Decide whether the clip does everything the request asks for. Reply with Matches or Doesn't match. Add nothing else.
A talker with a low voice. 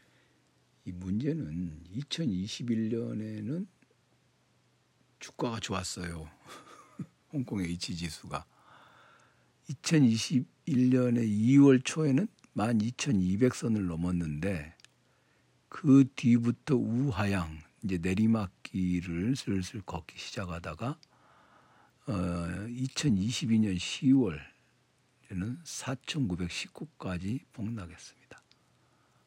Matches